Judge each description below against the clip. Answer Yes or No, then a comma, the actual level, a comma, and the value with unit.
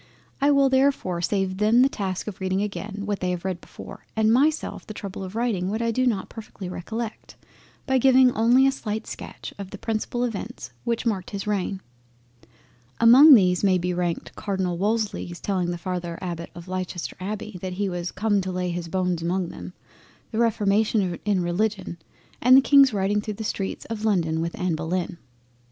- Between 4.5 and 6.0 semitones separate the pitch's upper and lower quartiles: No, average, 3.7 semitones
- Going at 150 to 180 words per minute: No, average, 190 wpm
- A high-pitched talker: Yes, high, 200 Hz